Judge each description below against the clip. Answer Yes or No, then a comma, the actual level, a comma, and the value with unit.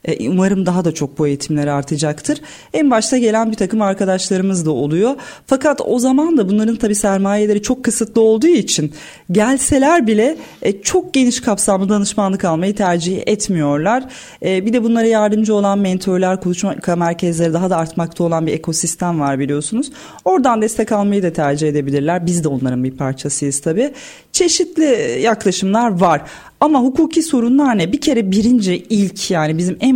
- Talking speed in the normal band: No, fast, 155 wpm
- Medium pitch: No, high, 200 Hz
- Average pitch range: No, wide, 6.2 semitones